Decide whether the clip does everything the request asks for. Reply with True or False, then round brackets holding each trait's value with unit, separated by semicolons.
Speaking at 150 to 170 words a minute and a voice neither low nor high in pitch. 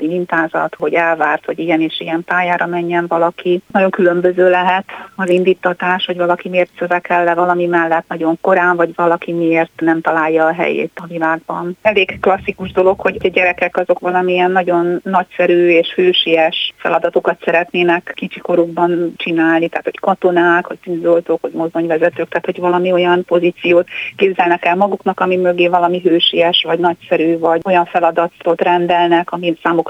True (155 wpm; 175 Hz)